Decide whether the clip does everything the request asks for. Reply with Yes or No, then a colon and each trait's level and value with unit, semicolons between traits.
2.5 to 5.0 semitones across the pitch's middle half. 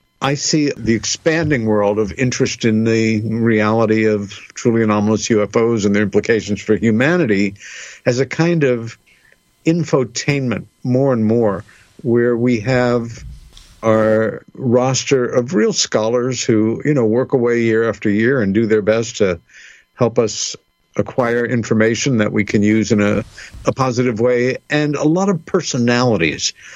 Yes: average, 2.9 semitones